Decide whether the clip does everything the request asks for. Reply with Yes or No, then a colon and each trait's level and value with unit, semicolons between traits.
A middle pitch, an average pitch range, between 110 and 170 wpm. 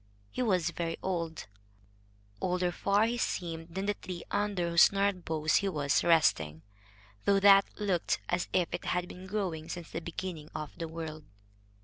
Yes: medium, 175 Hz; average, 3.2 semitones; average, 165 wpm